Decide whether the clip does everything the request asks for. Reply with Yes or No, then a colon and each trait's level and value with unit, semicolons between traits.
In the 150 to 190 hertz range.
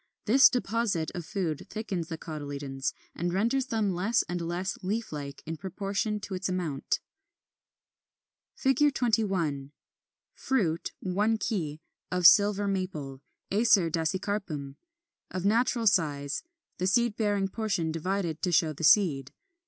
Yes: medium, 185 Hz